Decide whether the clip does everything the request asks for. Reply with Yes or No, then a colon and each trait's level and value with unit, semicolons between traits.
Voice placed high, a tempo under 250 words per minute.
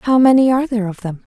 No: high, 230 Hz; fast, 265 wpm